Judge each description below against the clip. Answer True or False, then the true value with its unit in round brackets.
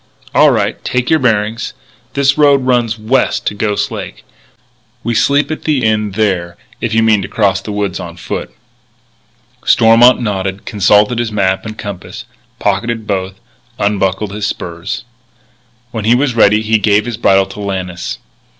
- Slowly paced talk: False (160 wpm)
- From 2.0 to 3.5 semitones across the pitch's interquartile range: True (3.1 semitones)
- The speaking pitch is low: True (105 Hz)